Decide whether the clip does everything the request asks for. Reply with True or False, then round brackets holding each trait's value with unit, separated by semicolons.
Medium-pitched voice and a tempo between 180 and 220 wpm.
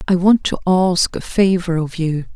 True (175 Hz; 205 wpm)